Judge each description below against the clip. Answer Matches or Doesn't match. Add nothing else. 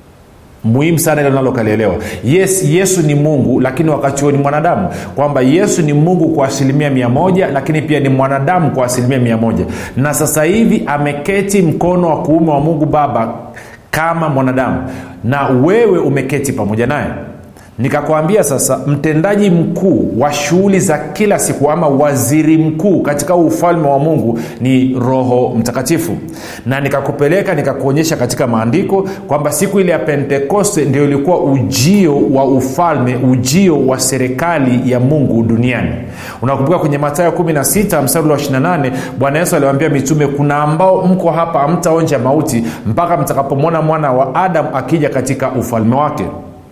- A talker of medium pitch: Matches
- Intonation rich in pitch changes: Doesn't match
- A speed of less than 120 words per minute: Doesn't match